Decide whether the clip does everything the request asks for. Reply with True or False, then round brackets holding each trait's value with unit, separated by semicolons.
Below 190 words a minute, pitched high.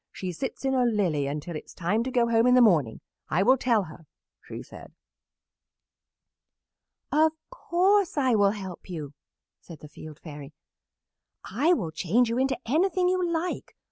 True (170 wpm; 225 Hz)